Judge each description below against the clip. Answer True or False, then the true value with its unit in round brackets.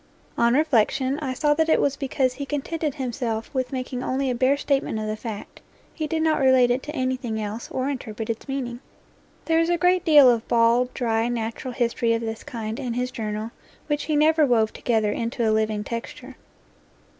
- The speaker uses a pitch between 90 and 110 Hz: False (250 Hz)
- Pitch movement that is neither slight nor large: True (3.7 semitones)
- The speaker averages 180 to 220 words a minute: True (200 wpm)